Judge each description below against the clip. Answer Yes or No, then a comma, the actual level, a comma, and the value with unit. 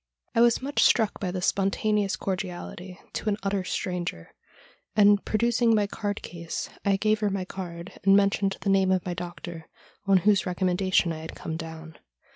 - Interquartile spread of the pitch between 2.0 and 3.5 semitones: Yes, narrow, 2.5 semitones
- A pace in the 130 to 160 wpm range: No, average, 180 wpm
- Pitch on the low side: No, high, 195 Hz